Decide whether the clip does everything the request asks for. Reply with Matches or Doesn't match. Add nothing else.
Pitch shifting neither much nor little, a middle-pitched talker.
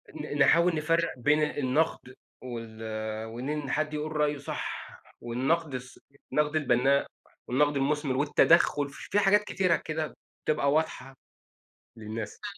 Matches